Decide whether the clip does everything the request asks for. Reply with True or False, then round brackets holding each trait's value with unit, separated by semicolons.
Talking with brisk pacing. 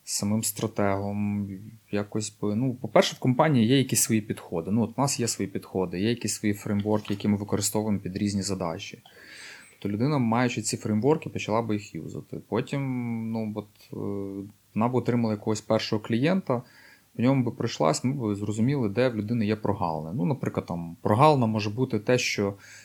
True (175 wpm)